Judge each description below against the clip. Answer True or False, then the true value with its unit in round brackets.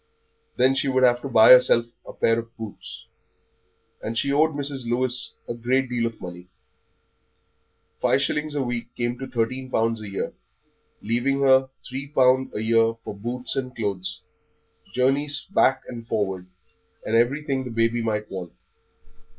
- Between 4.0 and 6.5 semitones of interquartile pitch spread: False (2.7 semitones)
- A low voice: True (120 Hz)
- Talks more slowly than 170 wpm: True (160 wpm)